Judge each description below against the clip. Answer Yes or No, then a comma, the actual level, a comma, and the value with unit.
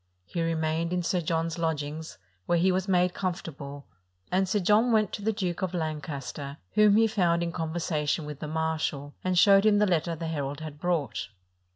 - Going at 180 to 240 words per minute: Yes, average, 190 wpm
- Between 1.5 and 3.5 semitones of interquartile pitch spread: Yes, average, 3.0 semitones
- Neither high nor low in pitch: Yes, medium, 165 Hz